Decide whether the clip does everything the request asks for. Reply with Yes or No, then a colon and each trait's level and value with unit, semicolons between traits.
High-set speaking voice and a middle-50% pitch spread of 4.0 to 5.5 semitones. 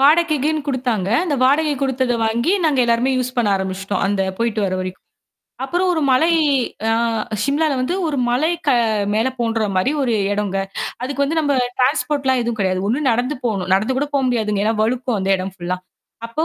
Yes: high, 245 Hz; average, 5.1 semitones